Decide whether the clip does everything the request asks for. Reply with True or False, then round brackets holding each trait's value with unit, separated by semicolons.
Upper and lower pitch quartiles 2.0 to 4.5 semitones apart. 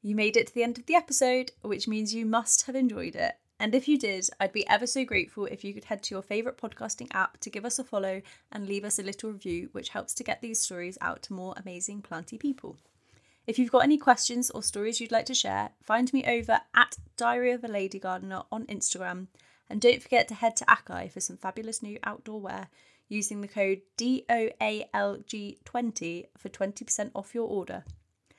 True (3.5 semitones)